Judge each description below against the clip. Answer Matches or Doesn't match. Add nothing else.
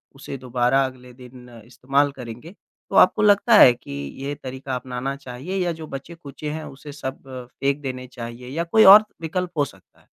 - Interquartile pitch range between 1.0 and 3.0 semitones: Doesn't match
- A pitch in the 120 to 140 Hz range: Matches